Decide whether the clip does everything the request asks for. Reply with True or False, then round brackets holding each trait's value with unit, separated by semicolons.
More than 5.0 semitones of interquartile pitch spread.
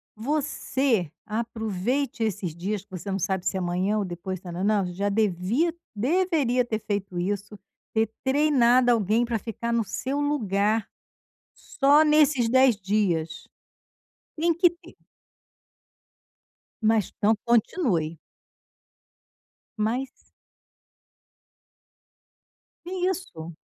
True (5.4 semitones)